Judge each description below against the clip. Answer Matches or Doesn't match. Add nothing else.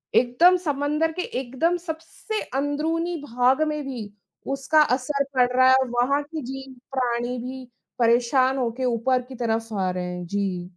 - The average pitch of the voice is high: Matches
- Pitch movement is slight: Doesn't match